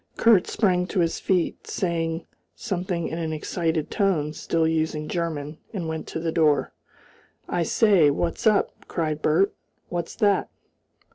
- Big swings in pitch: No, narrow, 2.5 semitones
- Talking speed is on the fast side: No, average, 145 wpm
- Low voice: No, medium, 165 Hz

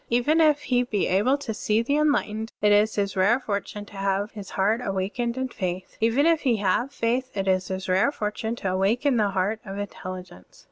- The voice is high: Yes, high, 210 Hz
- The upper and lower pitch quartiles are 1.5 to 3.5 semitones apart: No, average, 4.1 semitones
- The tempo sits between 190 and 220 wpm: Yes, fast, 205 wpm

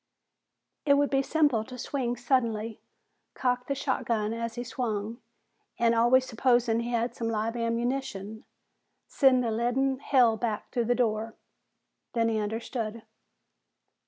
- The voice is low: No, high, 235 Hz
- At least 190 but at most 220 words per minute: No, slow, 135 wpm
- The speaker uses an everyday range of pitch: No, narrow, 2.2 semitones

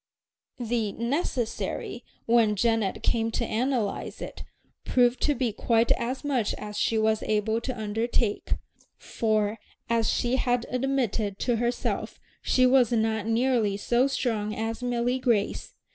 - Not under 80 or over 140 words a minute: Yes, slow, 135 wpm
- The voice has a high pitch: Yes, high, 230 Hz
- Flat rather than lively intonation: Yes, narrow, 2.2 semitones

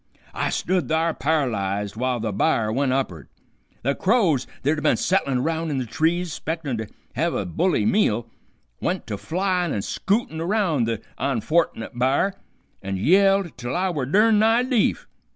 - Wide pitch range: Yes, wide, 7.3 semitones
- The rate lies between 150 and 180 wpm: Yes, average, 165 wpm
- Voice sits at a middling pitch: Yes, medium, 155 Hz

